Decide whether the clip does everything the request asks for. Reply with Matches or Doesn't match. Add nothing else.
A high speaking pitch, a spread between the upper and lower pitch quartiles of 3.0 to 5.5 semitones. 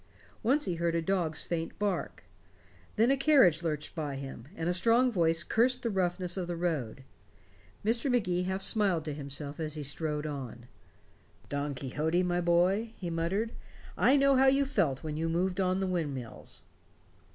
Doesn't match